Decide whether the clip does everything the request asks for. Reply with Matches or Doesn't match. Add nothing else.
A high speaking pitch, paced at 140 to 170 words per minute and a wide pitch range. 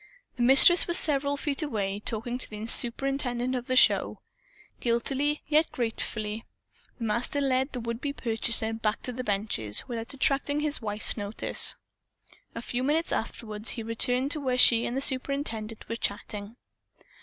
Doesn't match